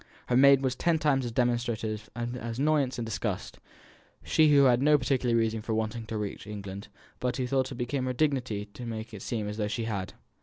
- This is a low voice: Yes, low, 120 Hz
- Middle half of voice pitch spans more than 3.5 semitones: No, average, 3.2 semitones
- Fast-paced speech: Yes, fast, 215 wpm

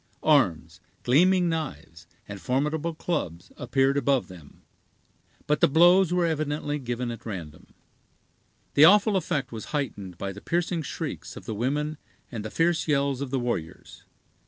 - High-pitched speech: No, medium, 140 Hz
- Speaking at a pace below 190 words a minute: Yes, average, 150 wpm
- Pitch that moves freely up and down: Yes, wide, 6.5 semitones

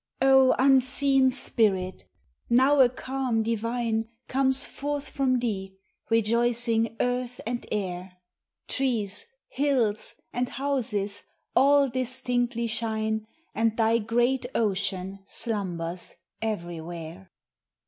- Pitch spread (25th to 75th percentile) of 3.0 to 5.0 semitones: Yes, average, 3.8 semitones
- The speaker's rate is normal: No, slow, 95 wpm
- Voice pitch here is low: No, high, 230 Hz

